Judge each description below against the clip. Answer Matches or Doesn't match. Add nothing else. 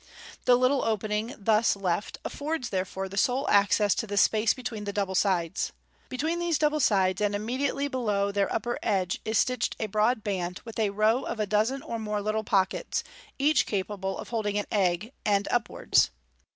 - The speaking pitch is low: Doesn't match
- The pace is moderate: Matches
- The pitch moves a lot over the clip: Doesn't match